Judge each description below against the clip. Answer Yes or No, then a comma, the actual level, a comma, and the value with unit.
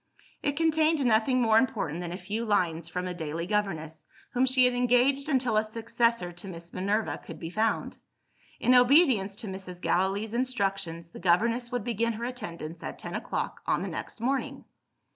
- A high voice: Yes, high, 220 Hz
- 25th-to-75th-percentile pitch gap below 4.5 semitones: No, wide, 5.5 semitones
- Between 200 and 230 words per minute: No, average, 180 wpm